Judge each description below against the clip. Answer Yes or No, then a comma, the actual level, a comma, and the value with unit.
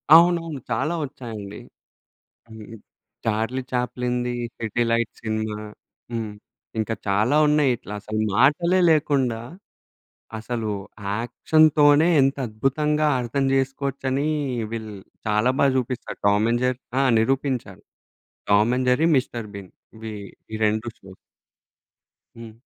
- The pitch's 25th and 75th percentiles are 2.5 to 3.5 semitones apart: No, average, 3.9 semitones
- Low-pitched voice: Yes, low, 120 Hz